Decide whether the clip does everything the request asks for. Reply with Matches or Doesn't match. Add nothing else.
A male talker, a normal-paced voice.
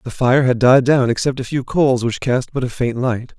Doesn't match